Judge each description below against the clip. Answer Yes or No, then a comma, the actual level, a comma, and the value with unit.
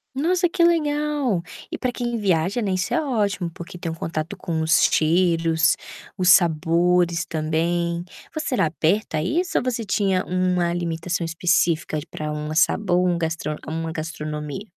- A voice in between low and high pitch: Yes, medium, 175 Hz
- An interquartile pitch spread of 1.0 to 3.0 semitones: No, average, 4.0 semitones